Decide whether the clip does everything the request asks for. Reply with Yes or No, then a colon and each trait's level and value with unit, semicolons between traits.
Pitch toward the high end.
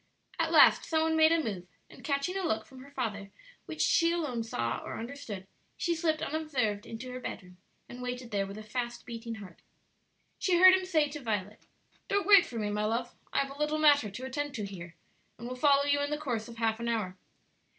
Yes: very high, 250 Hz